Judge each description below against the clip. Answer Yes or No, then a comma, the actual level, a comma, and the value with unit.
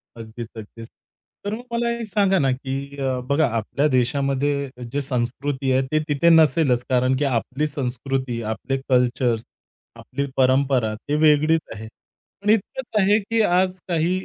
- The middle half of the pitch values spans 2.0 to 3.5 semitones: No, average, 4.0 semitones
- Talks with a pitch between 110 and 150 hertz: Yes, medium, 140 Hz